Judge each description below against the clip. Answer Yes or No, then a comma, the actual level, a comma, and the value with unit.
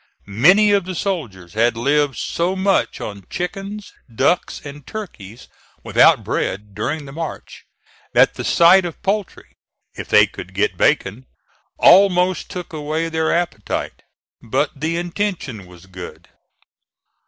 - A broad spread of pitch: Yes, wide, 8.7 semitones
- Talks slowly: Yes, slow, 130 wpm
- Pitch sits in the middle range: Yes, medium, 155 Hz